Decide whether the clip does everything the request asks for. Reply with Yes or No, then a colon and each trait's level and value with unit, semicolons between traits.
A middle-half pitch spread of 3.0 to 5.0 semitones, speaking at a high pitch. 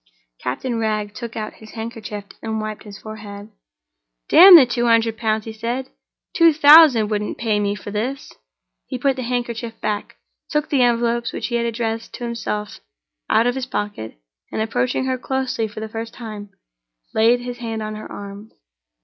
No: narrow, 2.4 semitones; high, 225 Hz